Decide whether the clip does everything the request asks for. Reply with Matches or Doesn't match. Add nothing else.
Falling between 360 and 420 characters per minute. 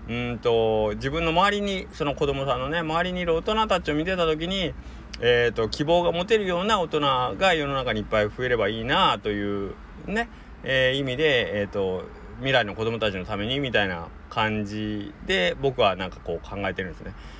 Matches